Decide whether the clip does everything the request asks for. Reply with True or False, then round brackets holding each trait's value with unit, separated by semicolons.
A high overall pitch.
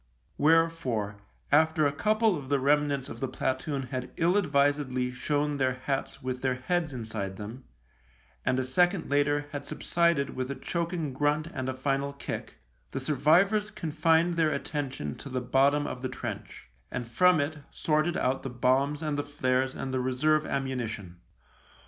False (140 Hz)